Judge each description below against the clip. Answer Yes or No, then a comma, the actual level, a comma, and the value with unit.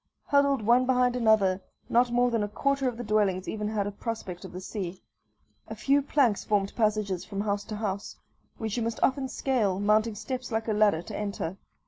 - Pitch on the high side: Yes, high, 215 Hz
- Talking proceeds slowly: No, average, 200 wpm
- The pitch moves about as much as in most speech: Yes, average, 3.4 semitones